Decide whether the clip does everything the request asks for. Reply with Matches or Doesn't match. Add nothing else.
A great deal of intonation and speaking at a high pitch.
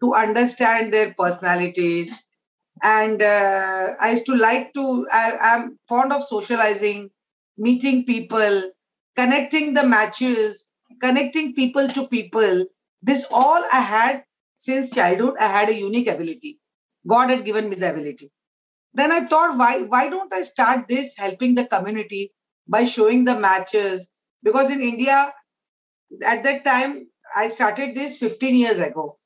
Doesn't match